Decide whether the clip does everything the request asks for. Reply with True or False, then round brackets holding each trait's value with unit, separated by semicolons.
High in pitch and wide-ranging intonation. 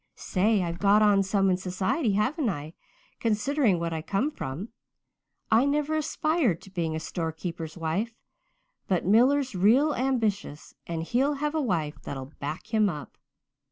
True (200 Hz; 7.2 semitones)